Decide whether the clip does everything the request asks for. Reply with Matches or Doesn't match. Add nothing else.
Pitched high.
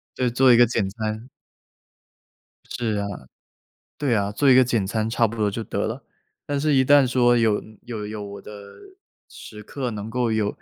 Doesn't match